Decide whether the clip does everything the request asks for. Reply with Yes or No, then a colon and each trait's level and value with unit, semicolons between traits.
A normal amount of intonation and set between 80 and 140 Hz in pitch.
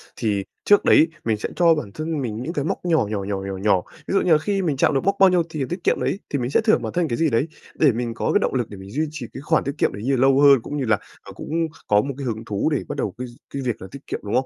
No: wide, 6.0 semitones; low, 135 Hz